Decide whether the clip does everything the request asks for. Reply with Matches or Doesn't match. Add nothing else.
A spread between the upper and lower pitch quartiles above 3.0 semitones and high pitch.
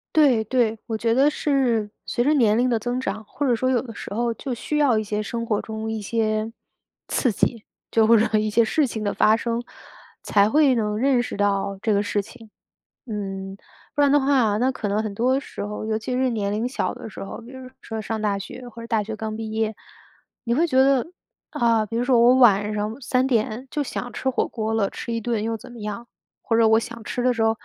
Doesn't match